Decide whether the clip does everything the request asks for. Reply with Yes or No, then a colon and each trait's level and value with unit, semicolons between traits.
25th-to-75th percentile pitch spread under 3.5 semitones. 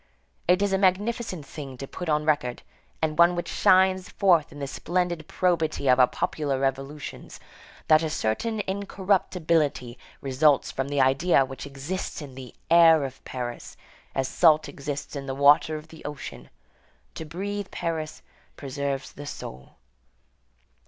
No: average, 4.6 semitones